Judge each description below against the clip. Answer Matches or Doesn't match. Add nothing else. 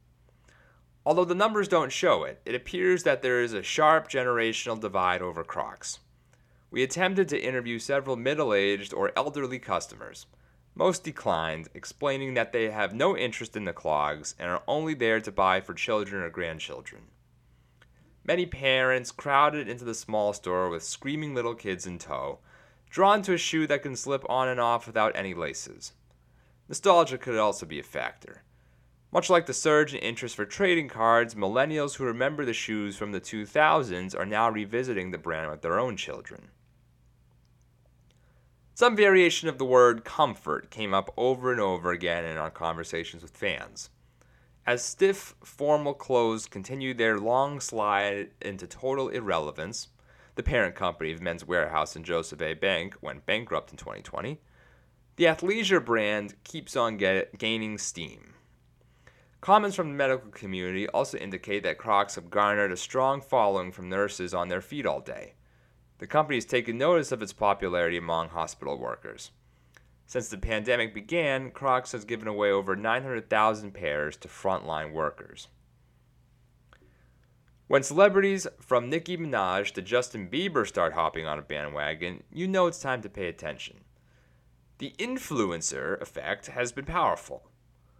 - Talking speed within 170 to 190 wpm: Doesn't match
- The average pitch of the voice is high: Doesn't match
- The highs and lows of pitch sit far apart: Matches